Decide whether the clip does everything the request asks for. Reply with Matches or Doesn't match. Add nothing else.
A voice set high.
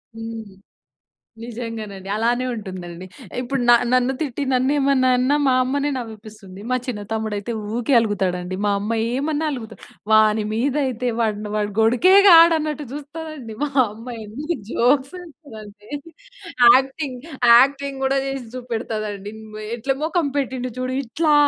Matches